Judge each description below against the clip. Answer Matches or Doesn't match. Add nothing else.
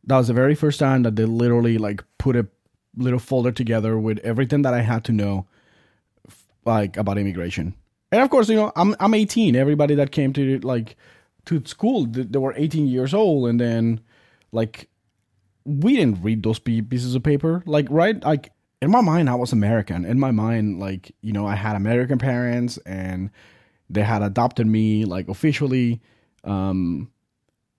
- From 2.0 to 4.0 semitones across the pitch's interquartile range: Doesn't match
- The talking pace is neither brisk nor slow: Matches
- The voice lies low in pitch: Matches